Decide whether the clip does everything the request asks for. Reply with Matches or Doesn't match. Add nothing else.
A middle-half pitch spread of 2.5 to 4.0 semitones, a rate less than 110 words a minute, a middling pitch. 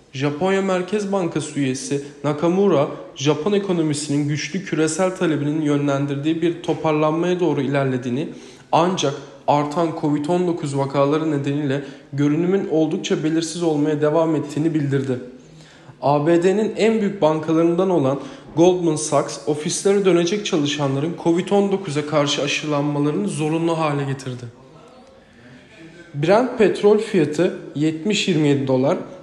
Matches